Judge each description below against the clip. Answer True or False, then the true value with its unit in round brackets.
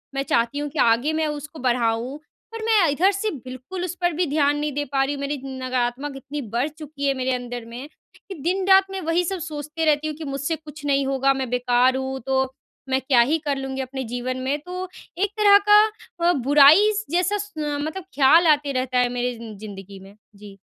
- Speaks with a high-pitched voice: True (280 Hz)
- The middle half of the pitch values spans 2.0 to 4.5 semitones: True (3.8 semitones)